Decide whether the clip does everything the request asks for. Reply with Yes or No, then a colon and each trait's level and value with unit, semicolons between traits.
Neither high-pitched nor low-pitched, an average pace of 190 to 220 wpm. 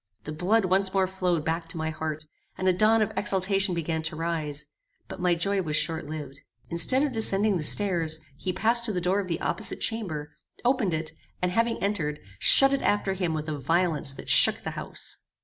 Yes: medium, 180 Hz; fast, 205 wpm